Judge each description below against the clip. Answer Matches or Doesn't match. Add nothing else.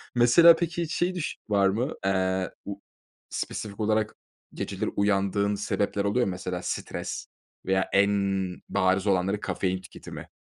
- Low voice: Matches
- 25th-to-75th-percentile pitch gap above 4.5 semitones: Doesn't match